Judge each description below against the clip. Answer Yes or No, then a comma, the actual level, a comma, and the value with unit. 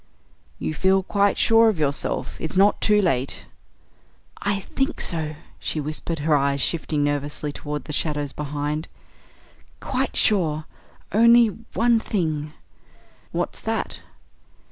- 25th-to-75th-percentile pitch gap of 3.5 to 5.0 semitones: No, wide, 5.5 semitones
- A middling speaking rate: No, slow, 130 wpm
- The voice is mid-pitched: Yes, medium, 155 Hz